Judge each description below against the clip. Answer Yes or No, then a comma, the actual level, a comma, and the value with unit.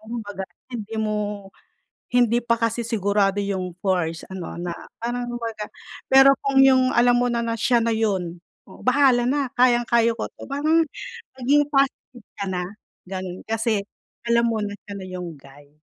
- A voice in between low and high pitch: No, high, 225 Hz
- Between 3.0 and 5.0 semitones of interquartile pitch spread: Yes, average, 3.8 semitones